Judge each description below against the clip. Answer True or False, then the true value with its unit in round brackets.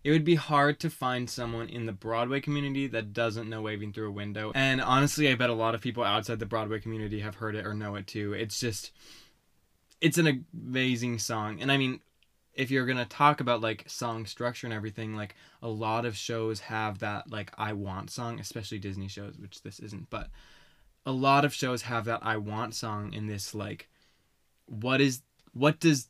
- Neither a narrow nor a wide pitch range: True (3.4 semitones)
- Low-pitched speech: True (115 Hz)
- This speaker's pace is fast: True (210 wpm)